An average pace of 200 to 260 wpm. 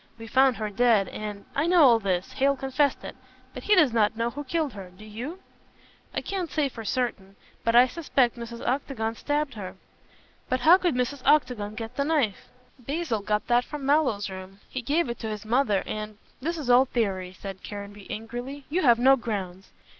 Yes: fast, 205 wpm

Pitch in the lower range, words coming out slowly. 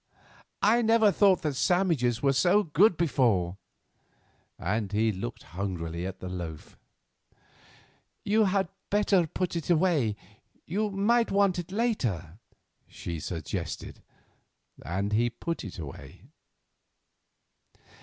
No: medium, 145 Hz; slow, 115 wpm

